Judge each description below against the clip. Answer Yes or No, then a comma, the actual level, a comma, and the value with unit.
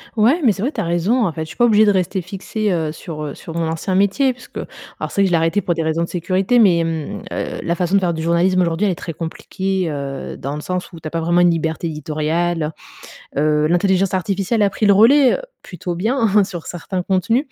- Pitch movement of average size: Yes, average, 3.5 semitones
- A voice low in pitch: No, medium, 180 Hz